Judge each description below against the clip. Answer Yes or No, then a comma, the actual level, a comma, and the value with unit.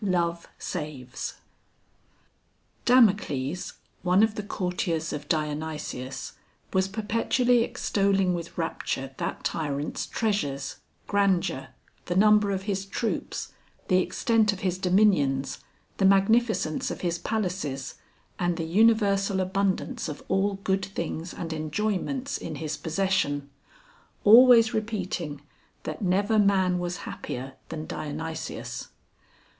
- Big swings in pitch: No, average, 4.6 semitones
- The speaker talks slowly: Yes, slow, 115 wpm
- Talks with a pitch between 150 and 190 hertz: Yes, medium, 185 Hz